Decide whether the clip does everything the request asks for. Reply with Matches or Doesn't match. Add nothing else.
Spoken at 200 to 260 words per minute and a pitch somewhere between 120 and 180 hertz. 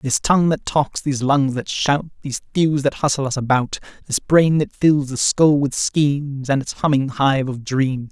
Matches